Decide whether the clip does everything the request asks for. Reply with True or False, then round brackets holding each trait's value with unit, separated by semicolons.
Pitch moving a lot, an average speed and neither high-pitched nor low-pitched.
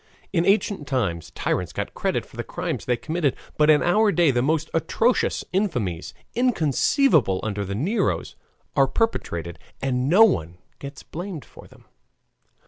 True (8.1 semitones; 150 wpm; 150 Hz)